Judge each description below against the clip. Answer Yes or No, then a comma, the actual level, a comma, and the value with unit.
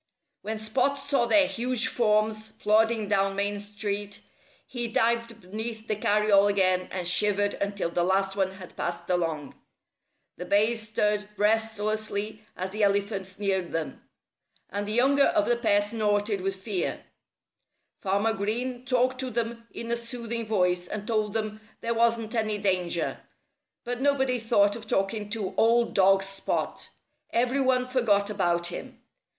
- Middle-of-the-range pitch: No, high, 215 Hz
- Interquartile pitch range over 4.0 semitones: No, average, 2.8 semitones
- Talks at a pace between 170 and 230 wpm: No, average, 150 wpm